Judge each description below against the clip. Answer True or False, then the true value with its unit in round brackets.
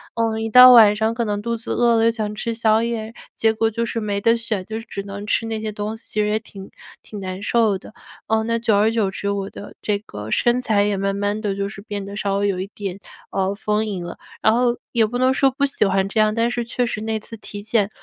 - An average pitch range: False (2.2 semitones)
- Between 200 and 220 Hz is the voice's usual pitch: True (215 Hz)